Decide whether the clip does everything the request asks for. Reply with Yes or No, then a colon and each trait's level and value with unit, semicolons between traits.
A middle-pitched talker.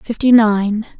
No: high, 220 Hz